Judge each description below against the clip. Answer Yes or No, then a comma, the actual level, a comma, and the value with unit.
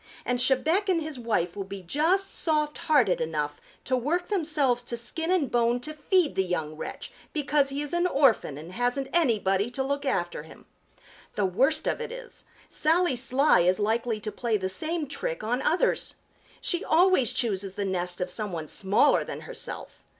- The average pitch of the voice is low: No, high, 245 Hz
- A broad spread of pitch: Yes, wide, 7.9 semitones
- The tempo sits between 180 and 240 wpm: Yes, average, 185 wpm